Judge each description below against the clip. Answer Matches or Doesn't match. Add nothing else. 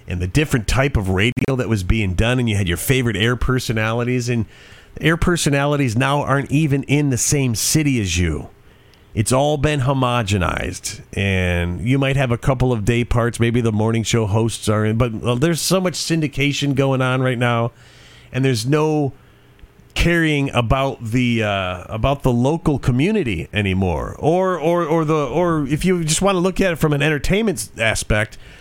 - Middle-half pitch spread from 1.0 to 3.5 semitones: Doesn't match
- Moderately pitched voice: Doesn't match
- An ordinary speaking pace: Matches